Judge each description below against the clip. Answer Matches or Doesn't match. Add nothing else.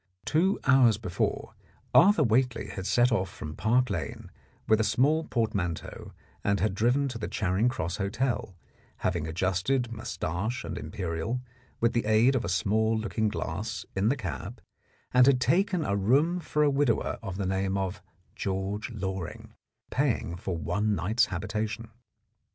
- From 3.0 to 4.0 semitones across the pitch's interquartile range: Doesn't match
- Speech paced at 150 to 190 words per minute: Matches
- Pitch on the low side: Matches